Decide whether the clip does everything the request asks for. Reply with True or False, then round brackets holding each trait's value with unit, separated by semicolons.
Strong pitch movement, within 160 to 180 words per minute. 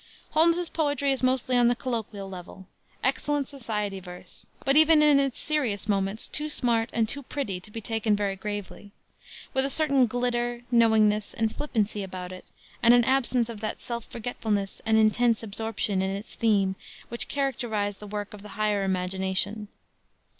False (3.8 semitones; 170 wpm)